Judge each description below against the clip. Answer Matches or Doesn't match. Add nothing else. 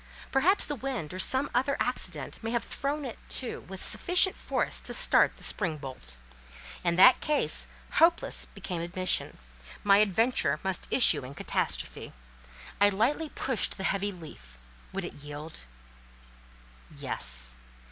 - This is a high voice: Matches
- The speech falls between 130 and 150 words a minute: Matches